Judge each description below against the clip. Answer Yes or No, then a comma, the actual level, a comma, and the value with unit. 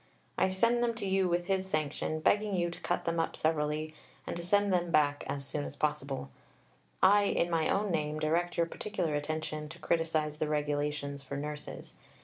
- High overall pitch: No, medium, 160 Hz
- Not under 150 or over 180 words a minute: No, average, 190 wpm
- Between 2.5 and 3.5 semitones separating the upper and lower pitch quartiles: Yes, average, 3.2 semitones